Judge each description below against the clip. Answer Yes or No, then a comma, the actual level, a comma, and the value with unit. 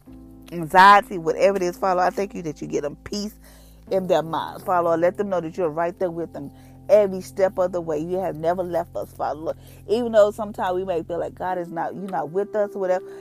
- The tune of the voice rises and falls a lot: No, average, 3.0 semitones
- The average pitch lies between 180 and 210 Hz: Yes, medium, 185 Hz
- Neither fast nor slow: No, fast, 240 wpm